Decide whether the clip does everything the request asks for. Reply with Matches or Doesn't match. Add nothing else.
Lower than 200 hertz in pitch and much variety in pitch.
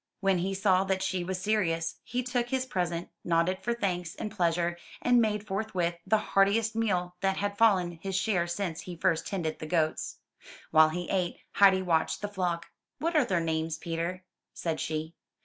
Doesn't match